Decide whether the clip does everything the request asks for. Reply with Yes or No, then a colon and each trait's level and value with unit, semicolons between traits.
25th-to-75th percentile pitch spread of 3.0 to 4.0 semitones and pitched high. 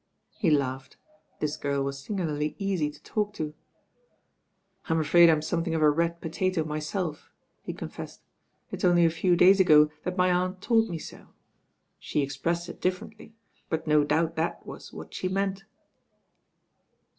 No: average, 3.4 semitones; medium, 165 Hz